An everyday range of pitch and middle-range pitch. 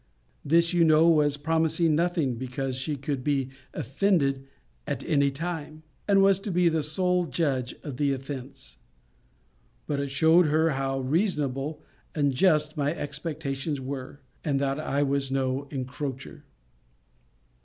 Yes: average, 3.1 semitones; medium, 145 Hz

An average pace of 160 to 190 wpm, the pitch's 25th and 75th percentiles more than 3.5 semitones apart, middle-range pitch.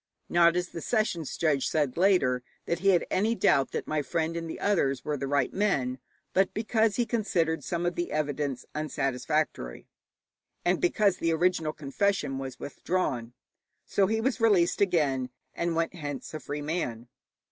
Yes: average, 170 wpm; average, 4.7 semitones; medium, 165 Hz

